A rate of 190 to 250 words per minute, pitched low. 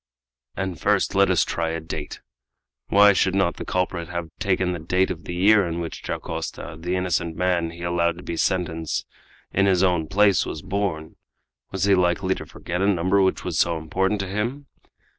Yes: average, 195 wpm; very low, 90 Hz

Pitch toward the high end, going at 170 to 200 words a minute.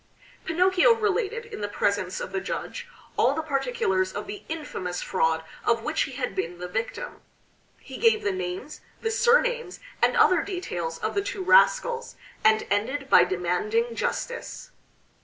No: very high, 275 Hz; average, 160 wpm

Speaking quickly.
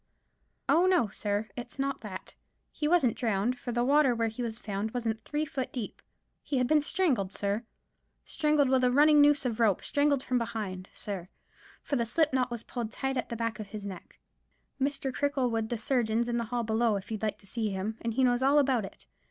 Yes: fast, 215 wpm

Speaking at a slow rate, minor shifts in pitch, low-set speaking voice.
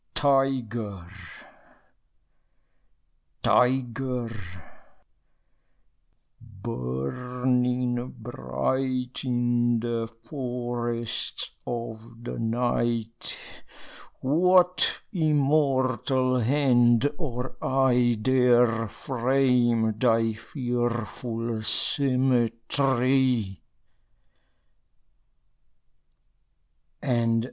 Yes: slow, 45 wpm; narrow, 2.1 semitones; low, 120 Hz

